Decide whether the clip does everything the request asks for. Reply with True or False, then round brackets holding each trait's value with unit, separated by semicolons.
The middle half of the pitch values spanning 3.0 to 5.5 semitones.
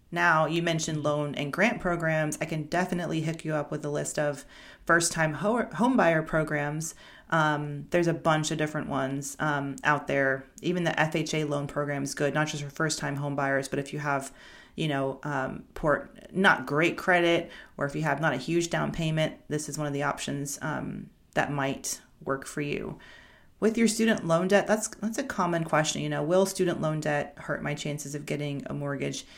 False (2.6 semitones)